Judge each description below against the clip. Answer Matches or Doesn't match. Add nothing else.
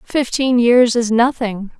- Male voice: Doesn't match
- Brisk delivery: Doesn't match